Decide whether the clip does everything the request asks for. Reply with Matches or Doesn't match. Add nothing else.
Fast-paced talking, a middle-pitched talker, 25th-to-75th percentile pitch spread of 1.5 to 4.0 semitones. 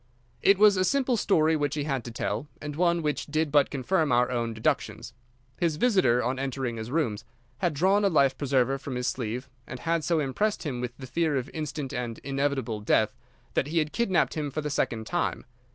Doesn't match